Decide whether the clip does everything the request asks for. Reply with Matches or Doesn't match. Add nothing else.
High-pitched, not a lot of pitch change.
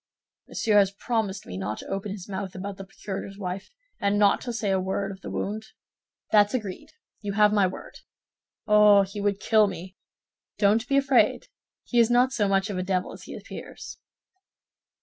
Matches